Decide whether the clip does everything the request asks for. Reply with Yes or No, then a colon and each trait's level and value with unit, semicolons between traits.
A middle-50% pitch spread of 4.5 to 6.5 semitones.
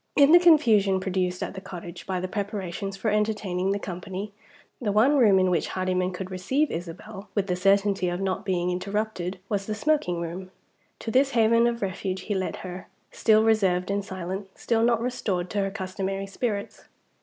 No: average, 2.8 semitones